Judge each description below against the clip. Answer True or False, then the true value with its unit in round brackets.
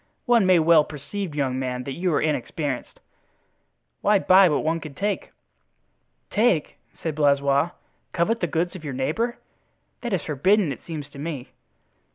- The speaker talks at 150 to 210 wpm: True (160 wpm)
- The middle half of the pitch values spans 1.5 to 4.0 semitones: False (4.8 semitones)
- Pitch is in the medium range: True (160 Hz)